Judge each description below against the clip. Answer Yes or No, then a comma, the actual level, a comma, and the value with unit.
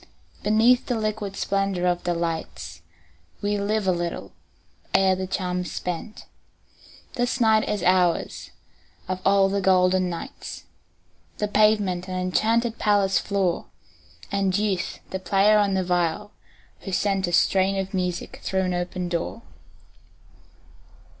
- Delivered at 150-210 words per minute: No, slow, 135 wpm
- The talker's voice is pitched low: No, high, 190 Hz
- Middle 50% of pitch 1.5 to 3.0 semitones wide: Yes, narrow, 2.4 semitones